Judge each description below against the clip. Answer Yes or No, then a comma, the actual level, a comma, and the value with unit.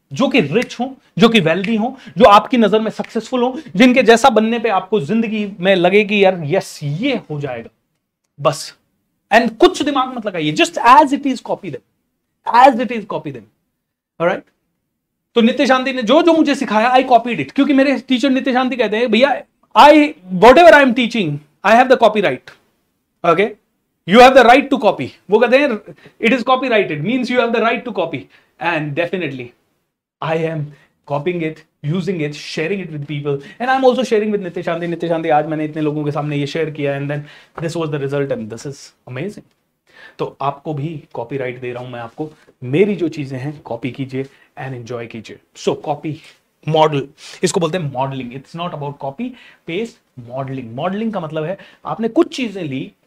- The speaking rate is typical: No, fast, 200 wpm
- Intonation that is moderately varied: No, wide, 8.5 semitones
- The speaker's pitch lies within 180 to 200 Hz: Yes, high, 190 Hz